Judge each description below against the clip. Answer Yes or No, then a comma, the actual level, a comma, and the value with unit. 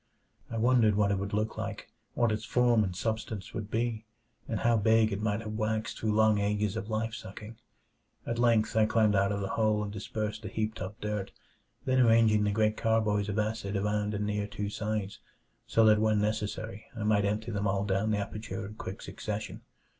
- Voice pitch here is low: Yes, low, 105 Hz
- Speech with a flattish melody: Yes, narrow, 1.3 semitones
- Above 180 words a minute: Yes, fast, 205 wpm